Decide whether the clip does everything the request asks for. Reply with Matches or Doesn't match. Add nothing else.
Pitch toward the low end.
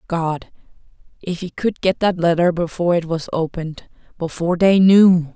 Doesn't match